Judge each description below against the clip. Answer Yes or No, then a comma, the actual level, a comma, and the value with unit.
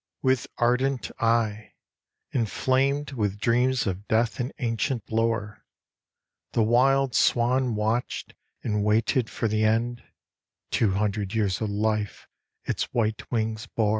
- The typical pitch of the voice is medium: No, low, 115 Hz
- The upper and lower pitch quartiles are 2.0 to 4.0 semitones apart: Yes, narrow, 2.6 semitones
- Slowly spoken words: Yes, slow, 125 wpm